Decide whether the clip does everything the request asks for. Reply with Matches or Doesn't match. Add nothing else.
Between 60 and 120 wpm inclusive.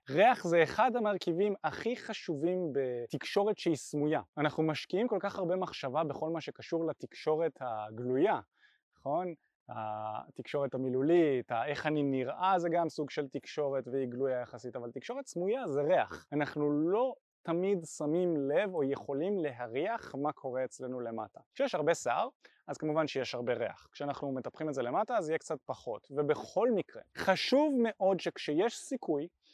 Doesn't match